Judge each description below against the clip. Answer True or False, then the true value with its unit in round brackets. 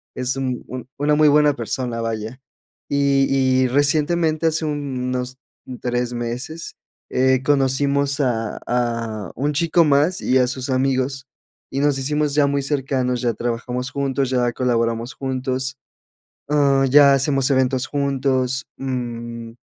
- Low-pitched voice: True (130 Hz)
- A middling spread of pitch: False (2.2 semitones)